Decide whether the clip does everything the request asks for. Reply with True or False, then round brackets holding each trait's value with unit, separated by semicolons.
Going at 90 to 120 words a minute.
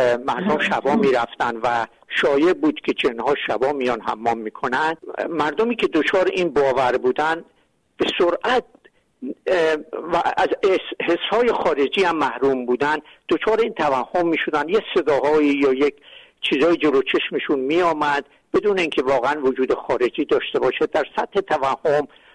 False (135 wpm)